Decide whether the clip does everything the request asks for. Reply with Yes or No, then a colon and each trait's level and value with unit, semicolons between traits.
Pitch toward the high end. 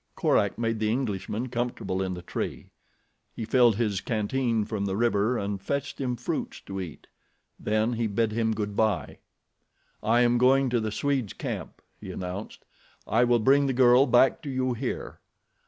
No: low, 115 Hz